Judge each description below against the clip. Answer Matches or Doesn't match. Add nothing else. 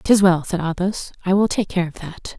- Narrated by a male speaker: Doesn't match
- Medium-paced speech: Doesn't match